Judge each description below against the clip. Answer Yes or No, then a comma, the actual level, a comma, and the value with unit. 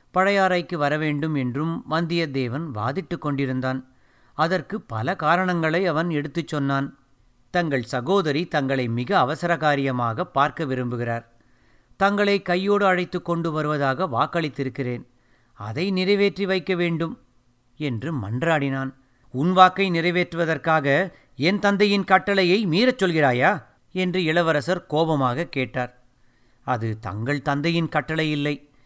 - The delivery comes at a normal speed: Yes, average, 100 wpm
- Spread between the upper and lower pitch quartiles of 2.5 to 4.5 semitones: No, average, 5.3 semitones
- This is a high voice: No, medium, 155 Hz